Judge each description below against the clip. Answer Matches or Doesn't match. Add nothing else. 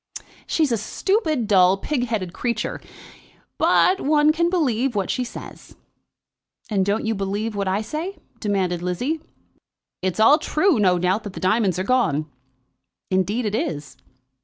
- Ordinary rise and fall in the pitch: Doesn't match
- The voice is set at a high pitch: Matches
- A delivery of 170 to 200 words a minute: Doesn't match